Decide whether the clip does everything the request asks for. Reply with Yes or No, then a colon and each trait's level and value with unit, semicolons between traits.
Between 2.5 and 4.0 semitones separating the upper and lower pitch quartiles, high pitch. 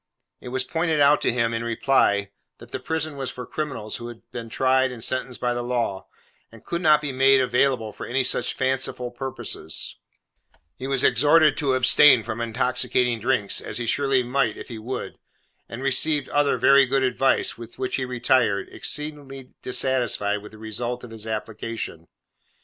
No: average, 2.8 semitones; low, 125 Hz